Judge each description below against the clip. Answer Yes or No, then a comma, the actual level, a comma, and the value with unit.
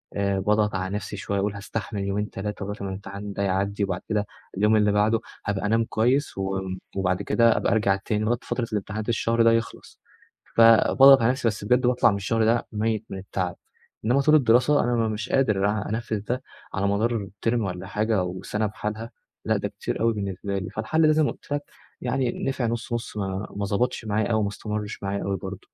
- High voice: No, low, 105 Hz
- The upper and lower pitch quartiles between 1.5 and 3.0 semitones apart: Yes, narrow, 2.6 semitones